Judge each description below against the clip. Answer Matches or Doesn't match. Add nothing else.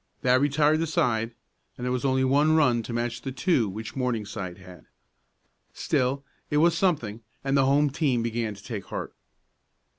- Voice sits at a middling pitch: Doesn't match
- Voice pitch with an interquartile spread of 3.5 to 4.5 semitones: Matches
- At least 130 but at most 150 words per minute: Doesn't match